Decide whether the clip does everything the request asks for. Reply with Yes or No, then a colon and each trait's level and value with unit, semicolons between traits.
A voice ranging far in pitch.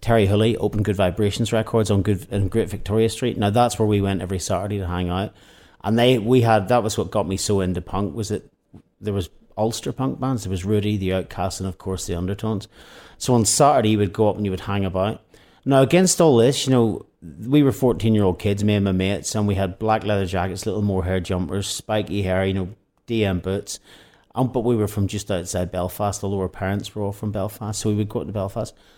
No: narrow, 2.6 semitones